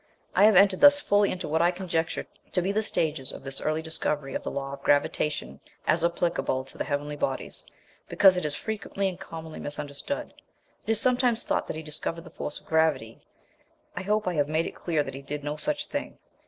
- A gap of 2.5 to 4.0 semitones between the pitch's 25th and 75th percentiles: No, average, 5.0 semitones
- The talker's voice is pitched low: No, medium, 160 Hz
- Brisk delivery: Yes, fast, 215 wpm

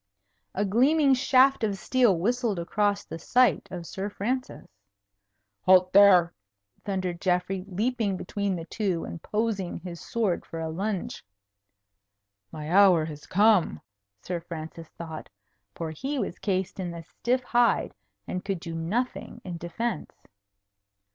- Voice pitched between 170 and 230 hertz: Yes, high, 190 Hz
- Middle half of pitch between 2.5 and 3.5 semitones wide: No, average, 4.5 semitones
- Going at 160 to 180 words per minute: No, slow, 135 wpm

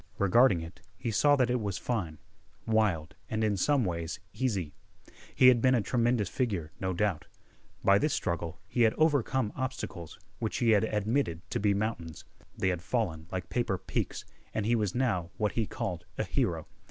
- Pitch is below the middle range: Yes, low, 105 Hz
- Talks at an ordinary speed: Yes, average, 180 wpm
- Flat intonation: No, average, 5.2 semitones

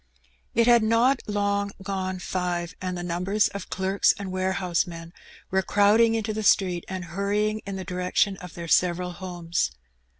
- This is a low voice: No, high, 190 Hz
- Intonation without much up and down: Yes, narrow, 2.3 semitones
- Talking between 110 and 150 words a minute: No, average, 160 wpm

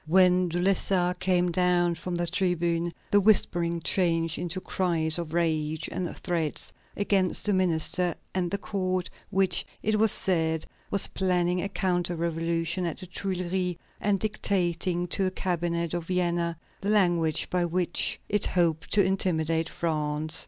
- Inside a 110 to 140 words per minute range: No, average, 150 wpm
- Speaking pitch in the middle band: Yes, medium, 175 Hz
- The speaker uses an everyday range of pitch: No, narrow, 1.9 semitones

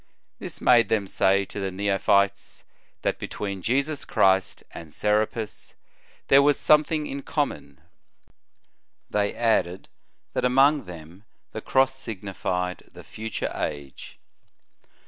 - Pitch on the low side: Yes, low, 105 Hz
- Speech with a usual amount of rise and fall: No, wide, 5.7 semitones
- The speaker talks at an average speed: No, slow, 120 wpm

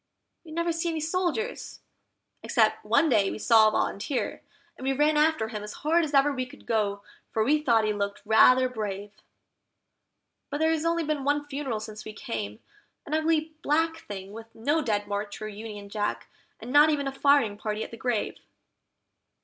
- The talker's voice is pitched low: No, very high, 255 Hz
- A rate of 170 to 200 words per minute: Yes, average, 185 wpm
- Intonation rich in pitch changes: Yes, wide, 6.3 semitones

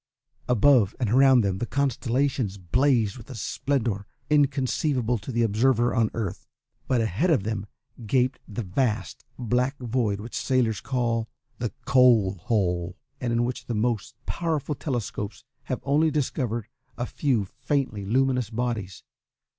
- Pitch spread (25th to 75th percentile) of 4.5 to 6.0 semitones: No, average, 3.7 semitones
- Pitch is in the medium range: No, low, 120 Hz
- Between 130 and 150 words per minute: Yes, average, 140 wpm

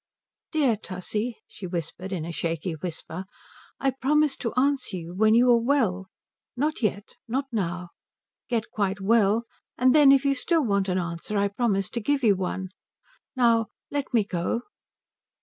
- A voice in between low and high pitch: No, high, 215 Hz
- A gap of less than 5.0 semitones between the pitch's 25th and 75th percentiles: No, wide, 5.4 semitones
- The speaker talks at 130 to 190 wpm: Yes, average, 165 wpm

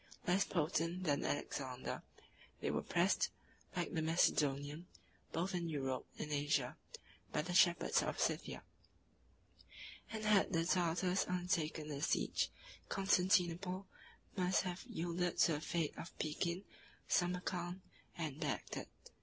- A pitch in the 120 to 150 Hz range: No, medium, 170 Hz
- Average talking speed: No, slow, 120 wpm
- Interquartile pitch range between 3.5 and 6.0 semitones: No, average, 3.1 semitones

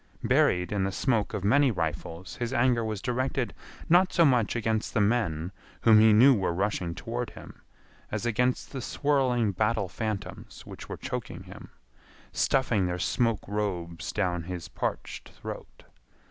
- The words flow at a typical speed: Yes, average, 155 wpm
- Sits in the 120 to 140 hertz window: No, low, 110 Hz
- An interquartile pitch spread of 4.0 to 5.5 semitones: Yes, average, 4.7 semitones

